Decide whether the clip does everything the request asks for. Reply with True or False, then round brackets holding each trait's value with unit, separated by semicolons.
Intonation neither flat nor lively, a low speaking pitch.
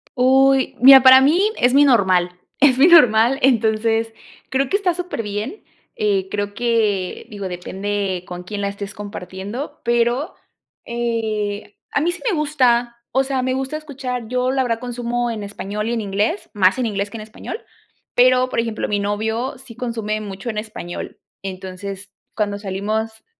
False (4.1 semitones; 230 Hz)